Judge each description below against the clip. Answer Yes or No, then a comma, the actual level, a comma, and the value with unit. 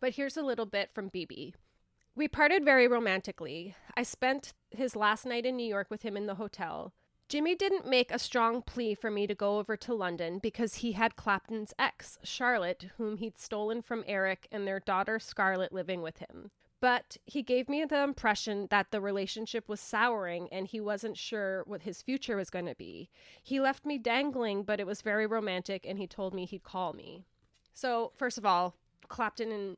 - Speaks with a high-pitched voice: Yes, high, 215 Hz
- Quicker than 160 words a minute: Yes, average, 195 wpm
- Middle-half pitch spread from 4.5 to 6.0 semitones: No, average, 3.8 semitones